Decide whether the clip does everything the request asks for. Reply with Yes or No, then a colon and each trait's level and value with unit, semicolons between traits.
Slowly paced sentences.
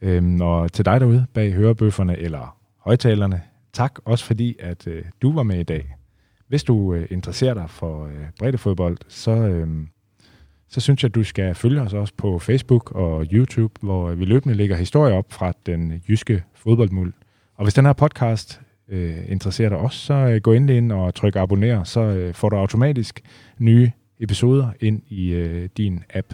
No: average, 185 wpm